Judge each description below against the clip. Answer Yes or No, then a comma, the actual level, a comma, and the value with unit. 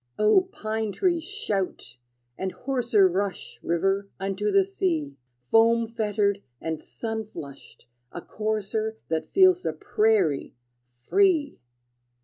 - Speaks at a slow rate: Yes, slow, 115 wpm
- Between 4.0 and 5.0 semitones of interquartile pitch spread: No, average, 3.3 semitones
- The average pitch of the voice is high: Yes, high, 210 Hz